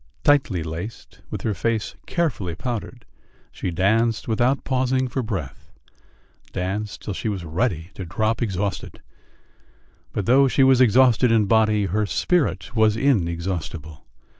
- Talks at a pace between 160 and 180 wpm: No, slow, 135 wpm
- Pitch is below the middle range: Yes, low, 110 Hz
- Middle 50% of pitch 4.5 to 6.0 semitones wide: Yes, average, 5.1 semitones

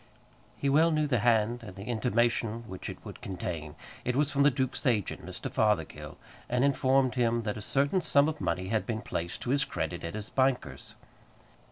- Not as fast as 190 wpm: No, average, 195 wpm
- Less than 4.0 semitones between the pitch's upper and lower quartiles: No, average, 4.6 semitones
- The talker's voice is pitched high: No, low, 120 Hz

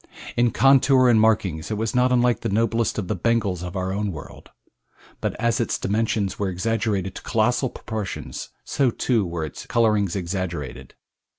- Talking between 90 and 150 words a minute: No, average, 170 wpm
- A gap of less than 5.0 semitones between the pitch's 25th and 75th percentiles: Yes, average, 3.9 semitones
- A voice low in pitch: Yes, low, 110 Hz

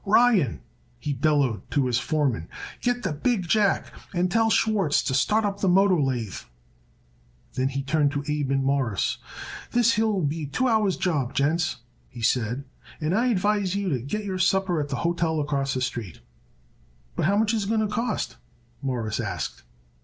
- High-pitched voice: No, medium, 160 Hz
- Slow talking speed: No, average, 185 wpm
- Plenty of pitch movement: Yes, wide, 7.0 semitones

